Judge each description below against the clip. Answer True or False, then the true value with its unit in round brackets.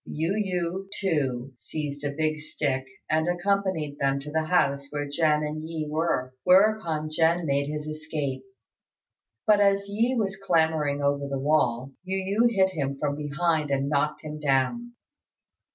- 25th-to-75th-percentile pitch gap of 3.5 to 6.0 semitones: True (4.3 semitones)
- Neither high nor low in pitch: True (155 Hz)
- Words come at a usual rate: True (155 wpm)